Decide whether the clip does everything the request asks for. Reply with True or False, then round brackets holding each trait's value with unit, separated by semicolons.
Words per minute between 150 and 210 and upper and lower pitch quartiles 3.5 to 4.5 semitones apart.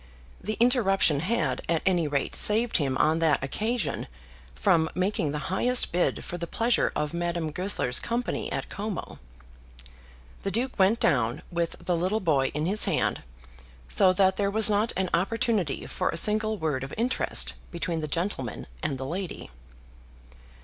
False (160 wpm; 5.4 semitones)